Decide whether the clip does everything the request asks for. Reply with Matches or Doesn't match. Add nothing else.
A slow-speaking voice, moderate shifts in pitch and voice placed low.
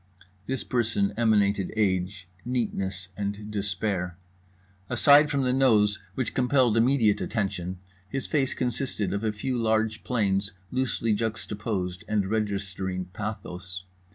Matches